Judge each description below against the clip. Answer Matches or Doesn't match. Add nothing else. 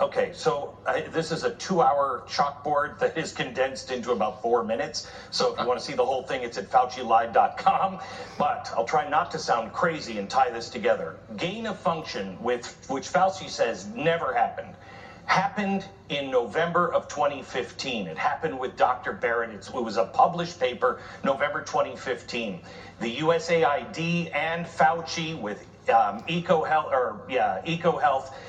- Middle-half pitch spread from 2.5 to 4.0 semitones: Doesn't match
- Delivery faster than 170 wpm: Doesn't match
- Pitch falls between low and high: Matches